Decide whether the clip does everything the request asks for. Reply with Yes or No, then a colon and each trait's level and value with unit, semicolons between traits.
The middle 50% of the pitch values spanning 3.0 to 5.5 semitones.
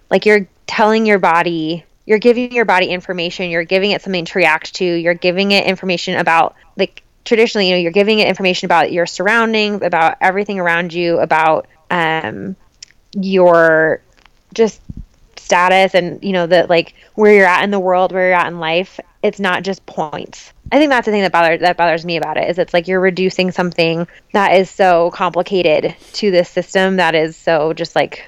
No: narrow, 2.4 semitones